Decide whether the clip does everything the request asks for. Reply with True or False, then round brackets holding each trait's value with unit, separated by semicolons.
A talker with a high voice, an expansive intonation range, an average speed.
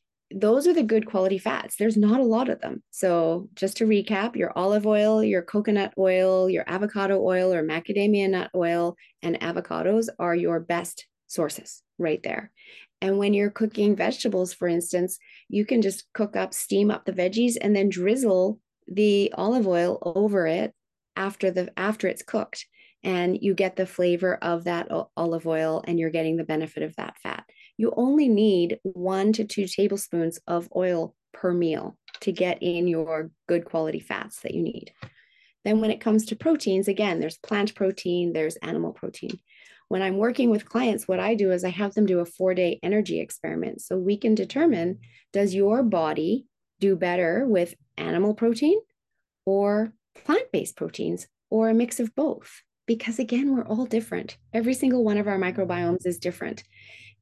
False (195 Hz; 3.6 semitones; 175 wpm)